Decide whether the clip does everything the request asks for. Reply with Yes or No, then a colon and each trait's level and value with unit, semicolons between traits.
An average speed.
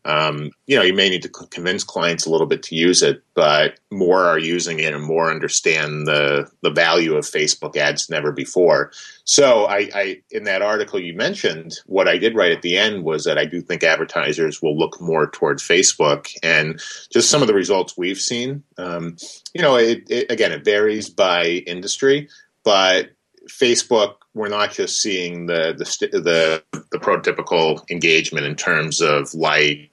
Yes: average, 180 wpm